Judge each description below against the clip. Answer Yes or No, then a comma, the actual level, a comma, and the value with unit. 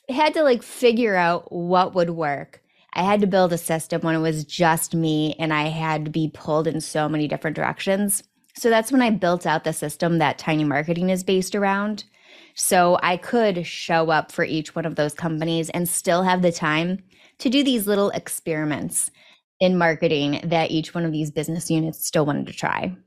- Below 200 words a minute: No, fast, 205 wpm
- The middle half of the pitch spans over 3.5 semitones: No, average, 3.2 semitones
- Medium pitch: Yes, medium, 170 Hz